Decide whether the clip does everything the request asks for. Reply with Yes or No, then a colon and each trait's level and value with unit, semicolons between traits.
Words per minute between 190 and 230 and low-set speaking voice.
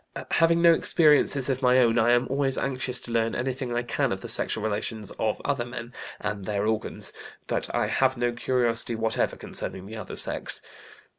Yes: average, 195 wpm; low, 120 Hz